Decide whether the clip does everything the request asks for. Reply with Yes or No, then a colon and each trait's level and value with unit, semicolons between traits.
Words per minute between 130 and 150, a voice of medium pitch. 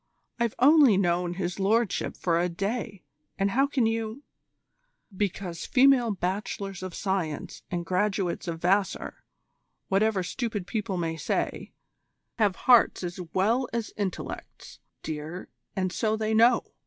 No: slow, 135 wpm; high, 195 Hz